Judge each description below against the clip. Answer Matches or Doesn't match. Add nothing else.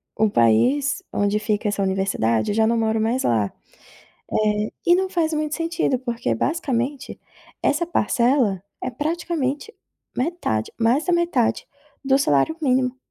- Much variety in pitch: Matches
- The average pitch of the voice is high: Matches